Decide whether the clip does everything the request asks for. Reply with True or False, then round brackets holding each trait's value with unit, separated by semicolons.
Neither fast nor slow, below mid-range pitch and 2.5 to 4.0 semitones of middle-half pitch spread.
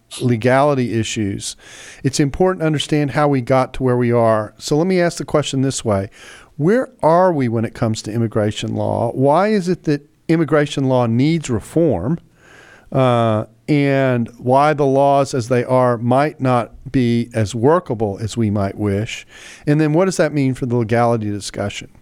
False (175 wpm; 130 Hz; 4.4 semitones)